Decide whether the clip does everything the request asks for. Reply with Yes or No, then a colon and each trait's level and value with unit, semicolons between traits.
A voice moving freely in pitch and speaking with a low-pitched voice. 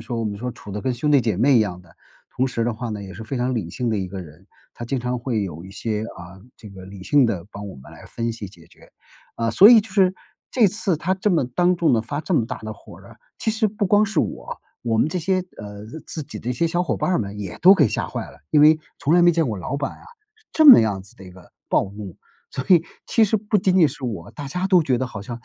Yes: wide, 8.7 semitones; low, 120 Hz